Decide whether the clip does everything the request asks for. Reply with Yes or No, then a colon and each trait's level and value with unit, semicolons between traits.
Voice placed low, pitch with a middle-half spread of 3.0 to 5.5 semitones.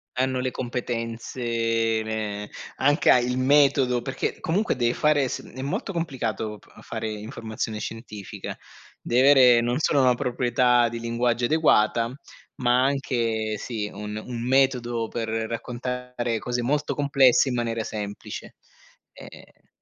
No: low, 120 Hz; narrow, 2.5 semitones